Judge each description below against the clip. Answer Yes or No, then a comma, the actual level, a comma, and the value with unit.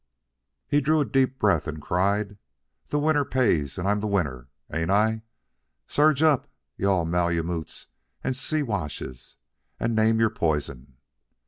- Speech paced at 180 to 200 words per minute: No, average, 140 wpm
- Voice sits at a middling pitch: No, low, 100 Hz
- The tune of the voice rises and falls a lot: Yes, wide, 7.8 semitones